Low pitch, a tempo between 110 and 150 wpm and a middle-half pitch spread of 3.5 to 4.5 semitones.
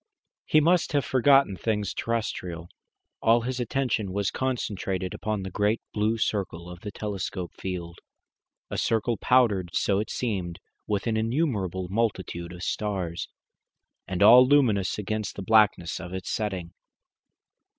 Yes: low, 105 Hz; average, 140 wpm; average, 3.9 semitones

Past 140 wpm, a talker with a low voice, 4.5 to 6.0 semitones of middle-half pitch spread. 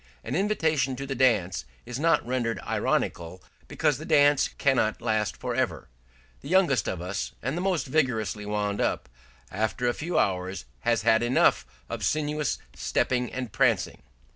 Yes: average, 160 wpm; low, 125 Hz; wide, 5.4 semitones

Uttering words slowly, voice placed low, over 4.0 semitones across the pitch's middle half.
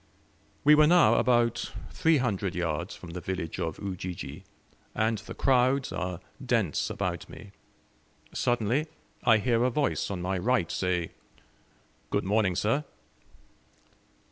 Yes: slow, 130 wpm; low, 105 Hz; wide, 5.4 semitones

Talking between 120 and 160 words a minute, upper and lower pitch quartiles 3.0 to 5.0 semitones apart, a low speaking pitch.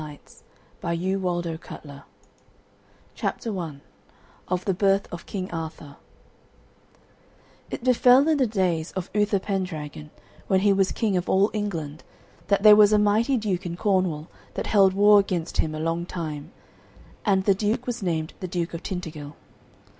No: average, 155 wpm; average, 3.8 semitones; medium, 185 Hz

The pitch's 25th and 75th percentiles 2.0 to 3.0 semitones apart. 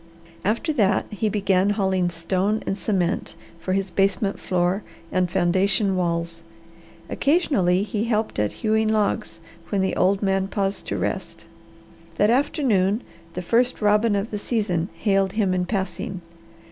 Yes: narrow, 2.6 semitones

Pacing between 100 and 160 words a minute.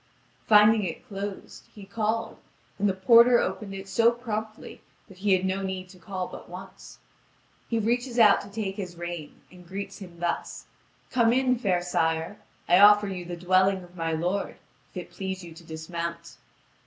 No: average, 180 wpm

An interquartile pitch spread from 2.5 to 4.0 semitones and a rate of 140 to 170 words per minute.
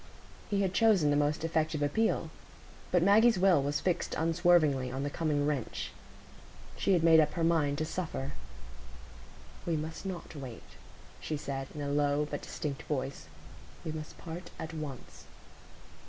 Yes: average, 3.0 semitones; average, 155 wpm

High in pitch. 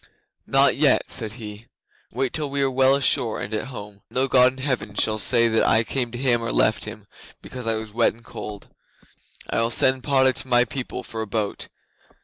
No: low, 120 Hz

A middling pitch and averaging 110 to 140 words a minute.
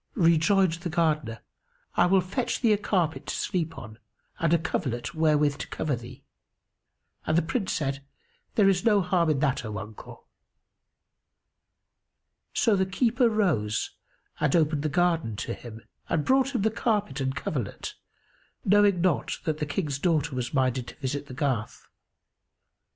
No: medium, 160 Hz; average, 155 wpm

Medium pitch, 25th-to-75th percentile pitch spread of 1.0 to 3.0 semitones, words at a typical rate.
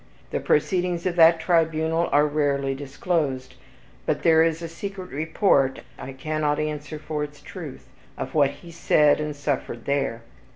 Yes: medium, 150 Hz; narrow, 2.6 semitones; average, 155 wpm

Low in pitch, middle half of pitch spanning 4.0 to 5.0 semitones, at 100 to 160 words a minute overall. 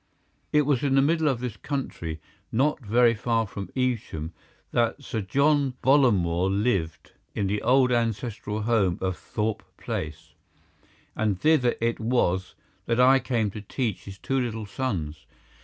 Yes: low, 115 Hz; average, 4.7 semitones; average, 150 wpm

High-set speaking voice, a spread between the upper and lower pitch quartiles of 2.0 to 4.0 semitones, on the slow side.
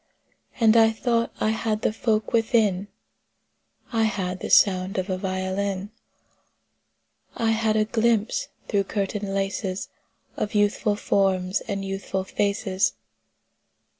Yes: high, 205 Hz; narrow, 2.4 semitones; slow, 120 wpm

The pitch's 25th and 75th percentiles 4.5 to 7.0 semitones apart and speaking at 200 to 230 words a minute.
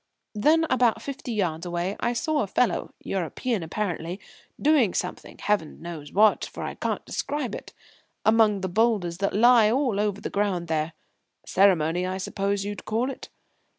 No: average, 4.8 semitones; average, 160 wpm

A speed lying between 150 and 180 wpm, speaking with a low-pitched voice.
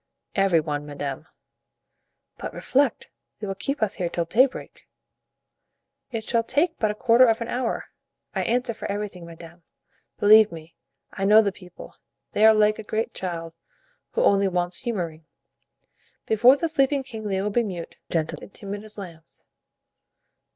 No: average, 160 wpm; high, 205 Hz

